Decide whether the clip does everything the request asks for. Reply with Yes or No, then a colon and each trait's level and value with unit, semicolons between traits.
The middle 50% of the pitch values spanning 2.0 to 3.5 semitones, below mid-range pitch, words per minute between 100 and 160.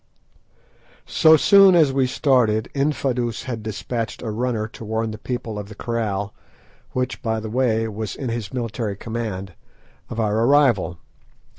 Yes: average, 2.9 semitones; low, 115 Hz; average, 150 wpm